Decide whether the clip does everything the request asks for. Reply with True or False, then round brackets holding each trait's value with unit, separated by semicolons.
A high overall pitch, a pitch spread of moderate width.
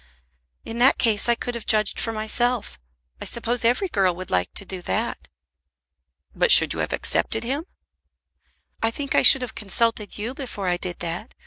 True (225 Hz; 3.6 semitones)